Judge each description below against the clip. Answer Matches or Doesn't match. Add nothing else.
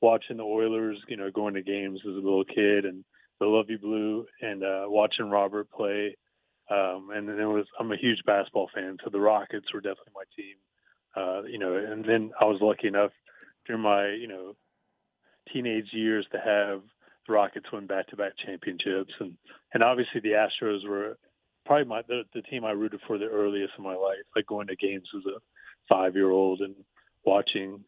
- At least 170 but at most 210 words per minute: Matches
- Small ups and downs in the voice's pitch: Matches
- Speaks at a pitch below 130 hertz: Matches